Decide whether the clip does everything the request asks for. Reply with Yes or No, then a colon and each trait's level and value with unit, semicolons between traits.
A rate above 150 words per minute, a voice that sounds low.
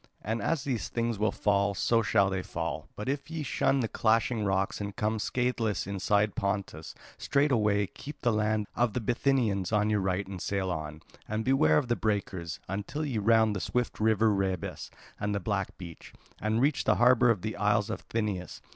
Yes: average, 190 wpm; low, 105 Hz